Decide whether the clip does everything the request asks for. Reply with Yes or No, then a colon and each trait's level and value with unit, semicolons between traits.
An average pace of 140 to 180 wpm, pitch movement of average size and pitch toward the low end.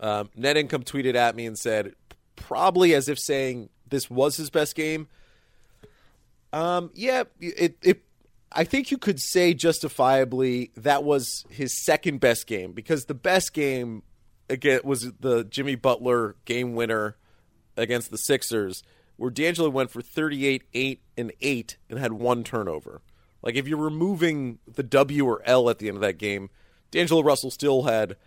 Yes: average, 165 wpm; average, 4.7 semitones; low, 130 Hz